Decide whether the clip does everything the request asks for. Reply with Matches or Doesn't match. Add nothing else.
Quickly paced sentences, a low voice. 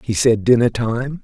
Doesn't match